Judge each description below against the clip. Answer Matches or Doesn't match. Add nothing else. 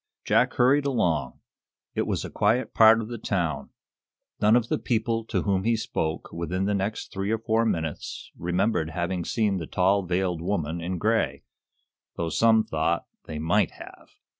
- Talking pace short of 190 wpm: Matches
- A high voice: Doesn't match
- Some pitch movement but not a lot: Matches